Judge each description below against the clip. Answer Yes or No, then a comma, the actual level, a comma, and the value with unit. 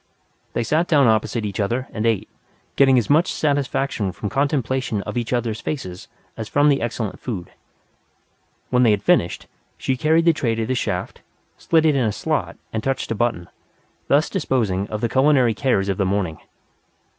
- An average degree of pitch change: Yes, average, 4.6 semitones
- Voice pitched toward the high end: No, low, 120 Hz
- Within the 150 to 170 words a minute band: No, average, 180 wpm